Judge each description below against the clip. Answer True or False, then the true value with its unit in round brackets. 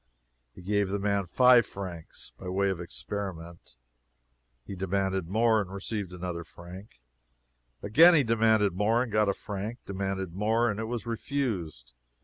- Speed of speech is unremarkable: True (150 wpm)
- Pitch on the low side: True (100 Hz)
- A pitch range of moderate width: True (3.4 semitones)